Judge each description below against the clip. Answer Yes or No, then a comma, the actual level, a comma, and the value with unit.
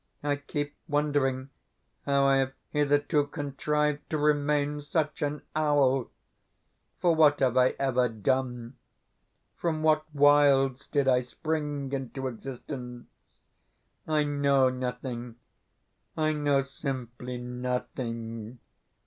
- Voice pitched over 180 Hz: No, medium, 140 Hz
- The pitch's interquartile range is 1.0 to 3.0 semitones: Yes, narrow, 2.5 semitones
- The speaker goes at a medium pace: No, slow, 105 wpm